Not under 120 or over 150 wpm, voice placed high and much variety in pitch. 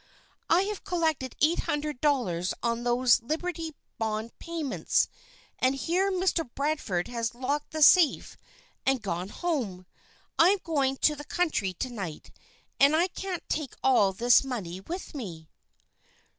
Yes: average, 140 wpm; very high, 270 Hz; wide, 6.0 semitones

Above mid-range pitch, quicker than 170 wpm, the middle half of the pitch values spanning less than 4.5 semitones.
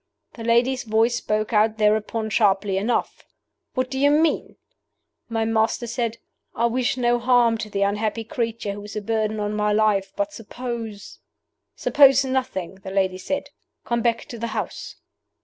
No: high, 225 Hz; average, 165 wpm; narrow, 2.4 semitones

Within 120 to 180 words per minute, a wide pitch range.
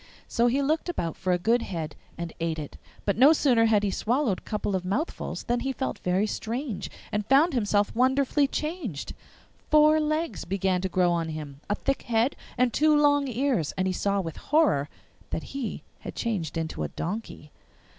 No: average, 190 wpm; wide, 7.2 semitones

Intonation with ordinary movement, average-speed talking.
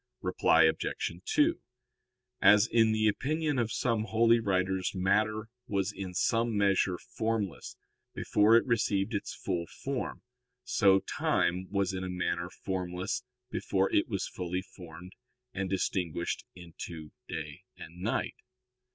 No: average, 3.4 semitones; slow, 130 wpm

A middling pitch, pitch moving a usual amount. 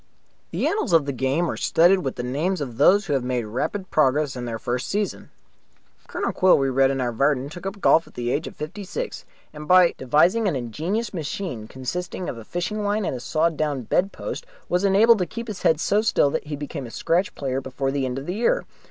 No: medium, 150 Hz; wide, 6.1 semitones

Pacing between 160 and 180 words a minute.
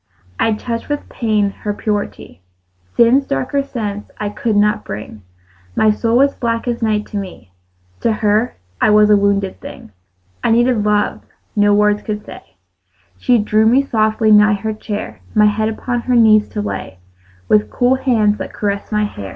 Yes: average, 175 wpm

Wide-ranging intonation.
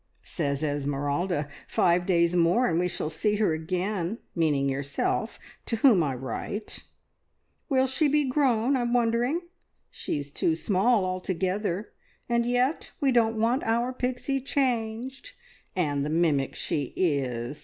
Yes: wide, 7.5 semitones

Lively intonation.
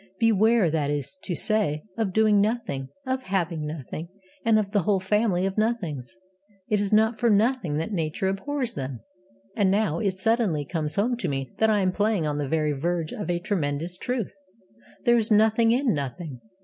Yes: wide, 5.9 semitones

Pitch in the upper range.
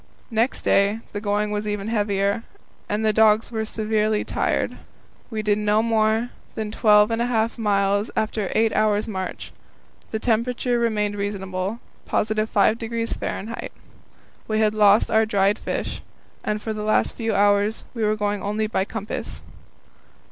Yes: high, 215 Hz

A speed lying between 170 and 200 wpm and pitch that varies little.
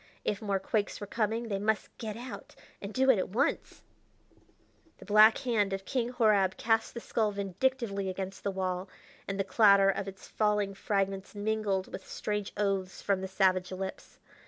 Yes: average, 175 wpm; narrow, 2.1 semitones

